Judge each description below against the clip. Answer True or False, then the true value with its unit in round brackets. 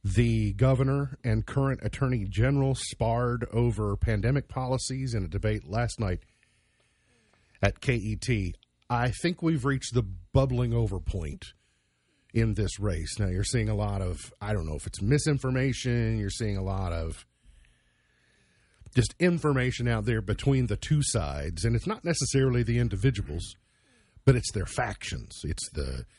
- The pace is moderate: True (150 wpm)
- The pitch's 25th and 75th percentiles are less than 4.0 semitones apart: False (4.3 semitones)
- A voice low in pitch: True (115 Hz)